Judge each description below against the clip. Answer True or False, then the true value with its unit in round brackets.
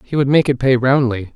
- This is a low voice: True (130 Hz)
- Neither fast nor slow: False (265 wpm)